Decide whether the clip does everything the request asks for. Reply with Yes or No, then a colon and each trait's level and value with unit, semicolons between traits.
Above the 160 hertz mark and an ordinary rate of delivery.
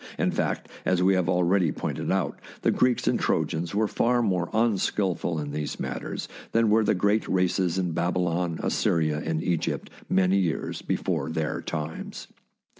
No: very low, 90 Hz; average, 160 wpm